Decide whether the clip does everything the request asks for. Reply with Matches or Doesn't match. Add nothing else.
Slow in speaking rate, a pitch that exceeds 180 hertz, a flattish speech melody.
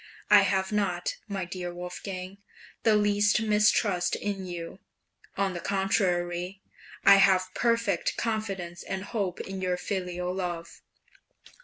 Matches